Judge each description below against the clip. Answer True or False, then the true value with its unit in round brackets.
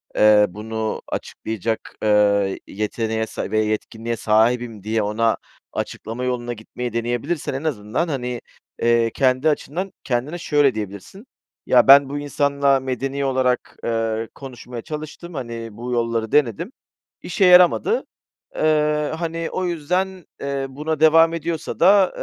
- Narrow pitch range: False (5.2 semitones)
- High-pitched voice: False (125 Hz)